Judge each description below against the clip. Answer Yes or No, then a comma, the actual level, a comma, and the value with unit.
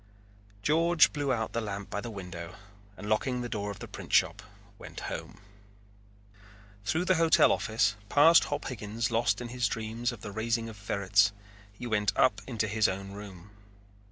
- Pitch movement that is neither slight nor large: Yes, average, 3.2 semitones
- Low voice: Yes, low, 110 Hz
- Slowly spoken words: No, average, 175 wpm